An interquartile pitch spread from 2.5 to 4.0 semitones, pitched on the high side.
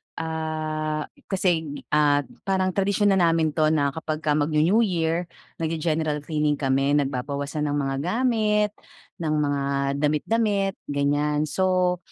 No: average, 3.6 semitones; medium, 155 Hz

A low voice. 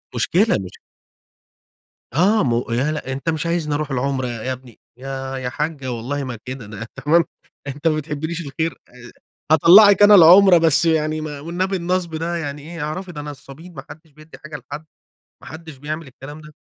No: medium, 150 Hz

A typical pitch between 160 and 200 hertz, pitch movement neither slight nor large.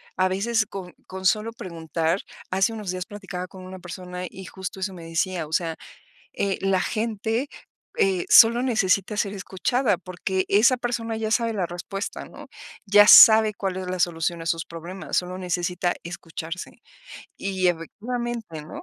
Yes: high, 190 Hz; average, 3.1 semitones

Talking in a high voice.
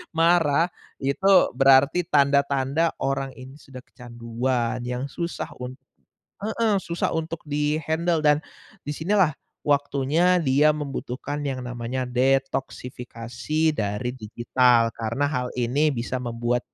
No: low, 135 Hz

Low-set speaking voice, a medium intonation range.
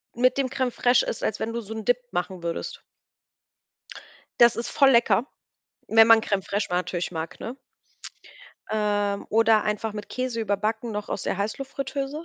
No: high, 220 Hz; average, 3.2 semitones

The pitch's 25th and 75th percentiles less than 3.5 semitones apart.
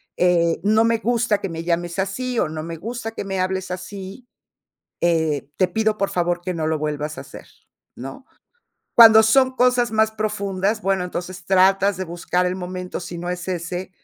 No: average, 3.8 semitones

